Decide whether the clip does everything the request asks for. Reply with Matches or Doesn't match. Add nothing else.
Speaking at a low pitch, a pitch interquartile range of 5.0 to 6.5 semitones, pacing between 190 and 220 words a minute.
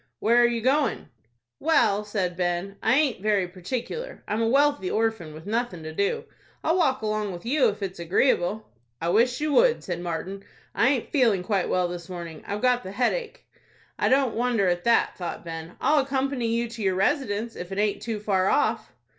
Doesn't match